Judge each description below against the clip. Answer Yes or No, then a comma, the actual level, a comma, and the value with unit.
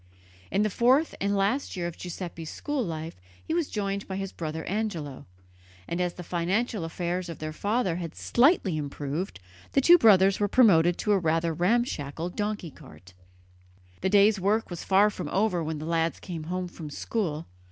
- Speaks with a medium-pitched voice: Yes, medium, 180 Hz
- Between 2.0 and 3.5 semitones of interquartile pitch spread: No, average, 4.2 semitones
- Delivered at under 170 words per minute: No, average, 180 wpm